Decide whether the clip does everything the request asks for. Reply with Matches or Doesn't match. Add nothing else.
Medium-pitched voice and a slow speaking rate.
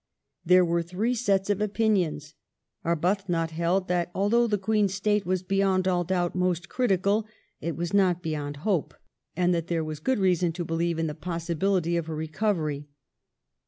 Doesn't match